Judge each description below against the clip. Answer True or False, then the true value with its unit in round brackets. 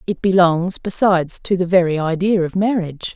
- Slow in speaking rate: False (170 wpm)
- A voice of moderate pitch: True (180 Hz)